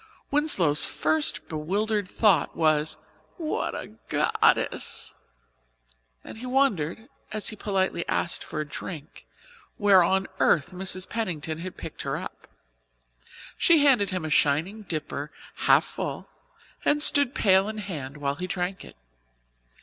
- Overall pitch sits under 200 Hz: Yes, medium, 185 Hz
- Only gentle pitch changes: No, wide, 5.4 semitones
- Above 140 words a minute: No, slow, 135 wpm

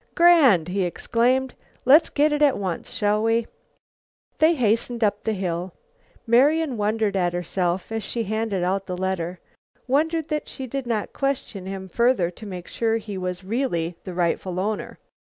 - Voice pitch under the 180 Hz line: No, high, 215 Hz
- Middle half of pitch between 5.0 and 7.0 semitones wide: Yes, wide, 5.6 semitones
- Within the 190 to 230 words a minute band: No, average, 165 wpm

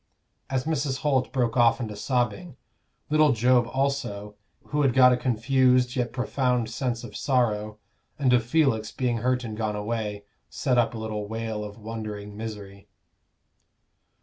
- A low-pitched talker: Yes, low, 120 Hz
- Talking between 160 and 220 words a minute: No, average, 150 wpm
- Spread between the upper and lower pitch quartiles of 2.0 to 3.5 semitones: Yes, average, 3.2 semitones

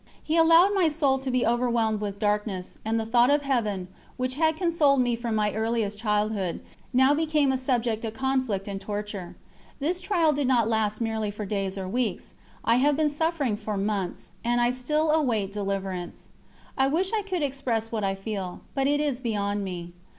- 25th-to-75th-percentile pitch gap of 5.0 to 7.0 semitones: Yes, average, 5.3 semitones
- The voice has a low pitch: No, high, 235 Hz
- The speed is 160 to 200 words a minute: Yes, average, 190 wpm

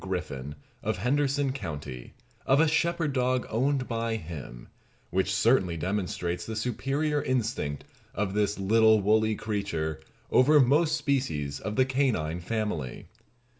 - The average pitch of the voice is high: No, low, 110 Hz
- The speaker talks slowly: Yes, slow, 130 wpm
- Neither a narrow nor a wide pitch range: No, wide, 7.0 semitones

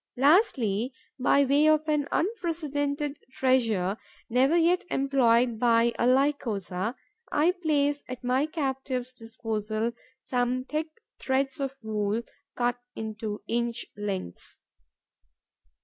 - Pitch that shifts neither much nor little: Yes, average, 4.1 semitones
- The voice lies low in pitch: No, very high, 255 Hz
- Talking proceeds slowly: Yes, slow, 105 wpm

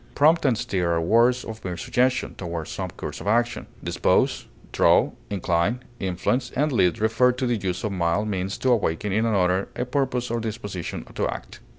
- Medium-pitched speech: No, low, 110 Hz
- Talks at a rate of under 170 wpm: No, average, 185 wpm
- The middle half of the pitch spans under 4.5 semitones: No, average, 5.2 semitones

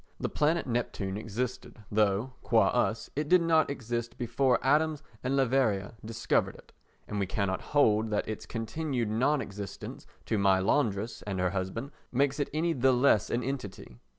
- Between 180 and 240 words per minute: No, average, 165 wpm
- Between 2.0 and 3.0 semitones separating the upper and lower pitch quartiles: No, average, 4.8 semitones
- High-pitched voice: No, low, 120 Hz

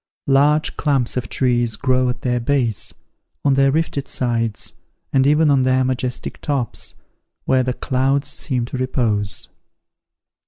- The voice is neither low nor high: No, low, 130 Hz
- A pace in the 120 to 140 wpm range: Yes, slow, 135 wpm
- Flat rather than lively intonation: Yes, narrow, 2.2 semitones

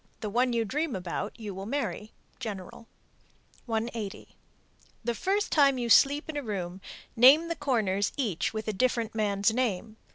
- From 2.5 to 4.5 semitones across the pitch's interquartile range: Yes, average, 4.2 semitones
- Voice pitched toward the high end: Yes, high, 225 Hz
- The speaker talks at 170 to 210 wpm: No, average, 160 wpm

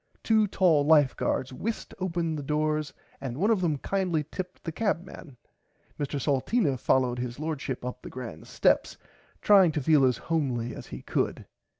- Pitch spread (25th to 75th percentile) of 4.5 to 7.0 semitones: Yes, average, 5.3 semitones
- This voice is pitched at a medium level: Yes, medium, 150 Hz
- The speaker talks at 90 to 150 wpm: No, average, 170 wpm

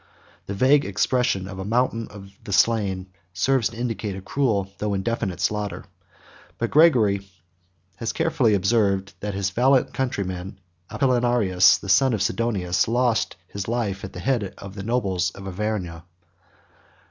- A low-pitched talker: Yes, low, 105 Hz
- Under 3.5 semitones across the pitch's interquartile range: No, average, 3.8 semitones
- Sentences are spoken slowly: No, average, 145 wpm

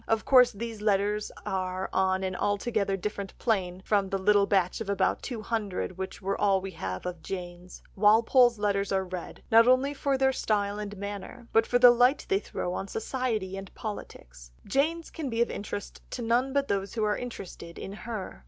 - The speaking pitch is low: No, high, 205 Hz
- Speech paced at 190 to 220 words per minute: Yes, average, 195 wpm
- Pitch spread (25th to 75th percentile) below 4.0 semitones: Yes, average, 3.5 semitones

